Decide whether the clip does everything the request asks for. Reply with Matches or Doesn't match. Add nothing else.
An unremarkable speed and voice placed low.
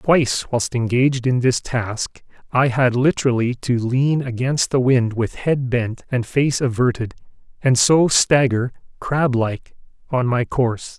Matches